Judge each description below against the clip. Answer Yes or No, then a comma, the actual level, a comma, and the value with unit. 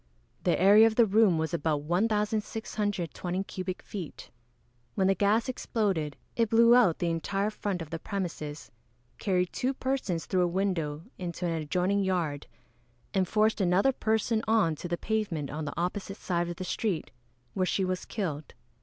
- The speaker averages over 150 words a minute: Yes, average, 165 wpm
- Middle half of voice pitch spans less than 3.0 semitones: No, average, 4.0 semitones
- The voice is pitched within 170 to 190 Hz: Yes, medium, 185 Hz